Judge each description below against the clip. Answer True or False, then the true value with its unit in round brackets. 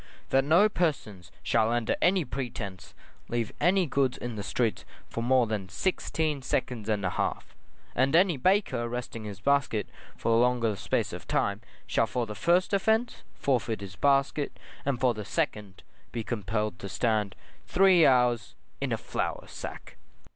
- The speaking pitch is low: True (120 Hz)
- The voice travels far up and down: False (4.9 semitones)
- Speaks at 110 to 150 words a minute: False (160 wpm)